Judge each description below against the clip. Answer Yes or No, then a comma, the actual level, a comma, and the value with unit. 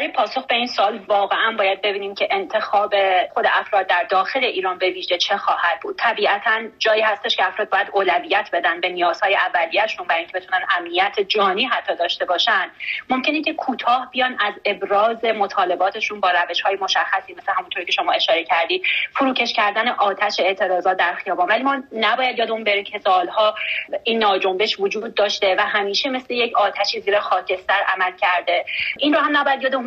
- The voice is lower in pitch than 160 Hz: No, high, 210 Hz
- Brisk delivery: Yes, fast, 175 wpm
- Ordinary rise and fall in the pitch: Yes, average, 4.3 semitones